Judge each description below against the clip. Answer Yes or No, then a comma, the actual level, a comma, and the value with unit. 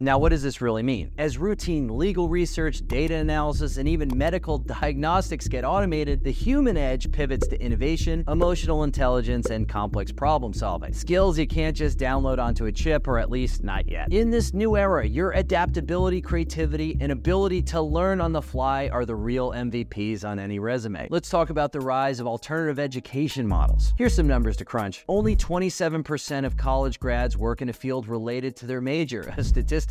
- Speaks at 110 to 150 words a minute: No, average, 185 wpm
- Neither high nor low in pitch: No, low, 130 Hz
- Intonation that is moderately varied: No, wide, 6.6 semitones